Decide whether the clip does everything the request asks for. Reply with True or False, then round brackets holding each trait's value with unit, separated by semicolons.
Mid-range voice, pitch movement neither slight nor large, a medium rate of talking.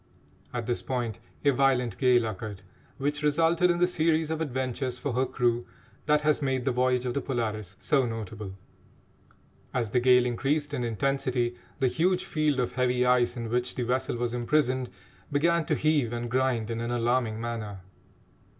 False (125 Hz; 3.1 semitones; 175 wpm)